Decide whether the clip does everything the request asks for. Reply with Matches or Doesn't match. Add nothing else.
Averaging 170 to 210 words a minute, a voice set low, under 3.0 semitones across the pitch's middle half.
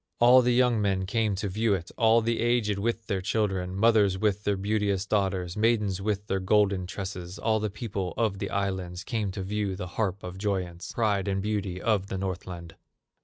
Matches